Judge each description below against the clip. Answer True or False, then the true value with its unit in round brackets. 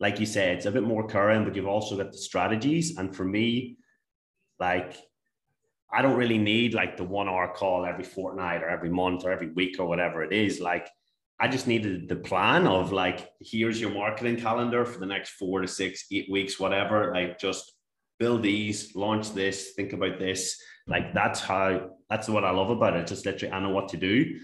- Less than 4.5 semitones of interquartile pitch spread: True (2.6 semitones)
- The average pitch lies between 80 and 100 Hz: True (95 Hz)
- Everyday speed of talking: False (210 wpm)